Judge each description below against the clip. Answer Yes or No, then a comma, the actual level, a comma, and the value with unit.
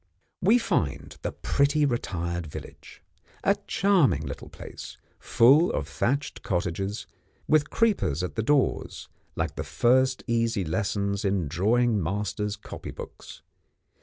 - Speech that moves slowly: Yes, slow, 120 wpm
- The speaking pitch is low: Yes, low, 110 Hz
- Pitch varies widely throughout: Yes, wide, 6.4 semitones